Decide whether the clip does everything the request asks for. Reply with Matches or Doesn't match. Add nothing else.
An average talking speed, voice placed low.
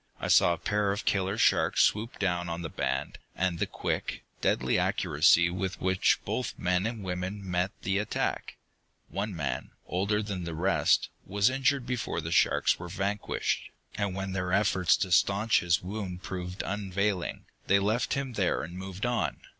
Matches